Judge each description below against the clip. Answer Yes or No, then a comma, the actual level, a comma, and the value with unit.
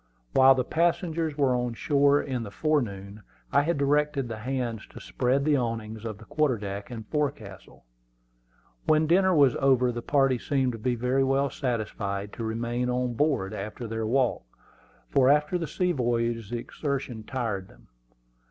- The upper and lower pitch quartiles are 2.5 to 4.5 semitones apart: Yes, average, 4.0 semitones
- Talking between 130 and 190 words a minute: Yes, average, 170 wpm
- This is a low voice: Yes, low, 125 Hz